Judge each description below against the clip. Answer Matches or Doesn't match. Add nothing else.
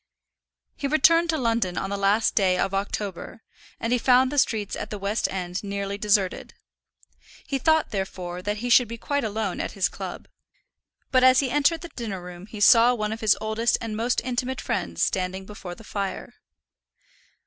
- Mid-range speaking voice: Doesn't match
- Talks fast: Doesn't match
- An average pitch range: Matches